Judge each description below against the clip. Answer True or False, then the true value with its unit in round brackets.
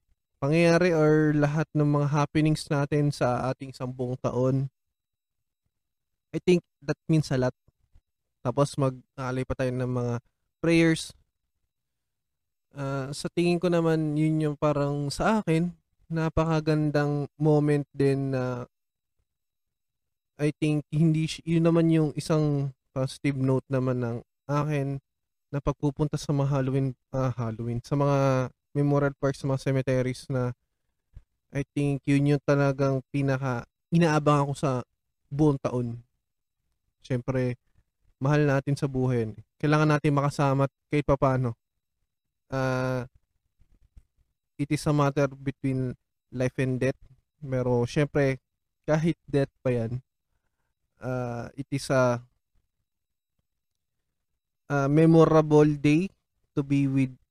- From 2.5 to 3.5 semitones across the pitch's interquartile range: True (2.8 semitones)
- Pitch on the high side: False (140 Hz)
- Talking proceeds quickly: False (120 wpm)